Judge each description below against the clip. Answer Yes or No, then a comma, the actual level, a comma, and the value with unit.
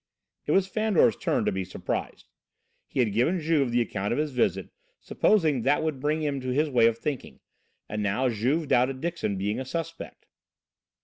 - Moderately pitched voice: No, low, 130 Hz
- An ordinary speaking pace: Yes, average, 185 wpm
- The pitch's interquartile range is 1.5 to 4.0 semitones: No, average, 5.3 semitones